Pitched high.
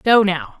Yes: high, 205 Hz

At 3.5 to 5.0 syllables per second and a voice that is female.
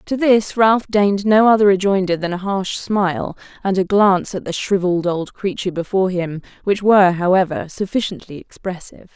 No: 5.5 syllables/s; female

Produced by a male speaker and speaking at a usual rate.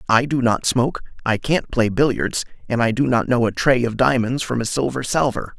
No: male; fast, 225 wpm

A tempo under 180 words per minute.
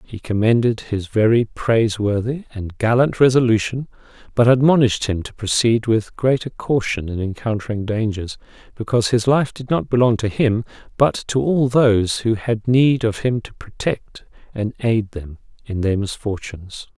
Yes: average, 155 wpm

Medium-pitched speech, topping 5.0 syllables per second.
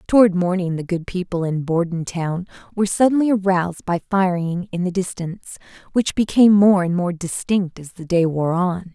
Yes: medium, 180 Hz; 5.3 syllables/s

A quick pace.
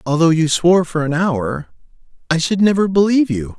No: average, 185 wpm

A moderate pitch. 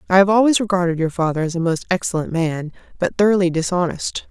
Yes: medium, 180 Hz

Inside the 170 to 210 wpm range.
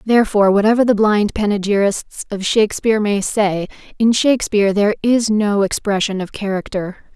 No: average, 145 wpm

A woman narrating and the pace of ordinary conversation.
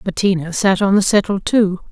Yes: female; average, 190 wpm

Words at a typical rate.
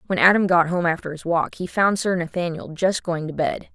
No: fast, 240 wpm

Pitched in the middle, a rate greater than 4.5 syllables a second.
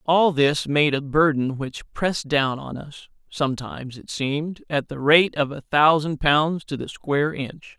No: medium, 150 Hz; 4.4 syllables/s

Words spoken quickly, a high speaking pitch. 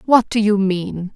Yes: fast, 210 wpm; high, 205 Hz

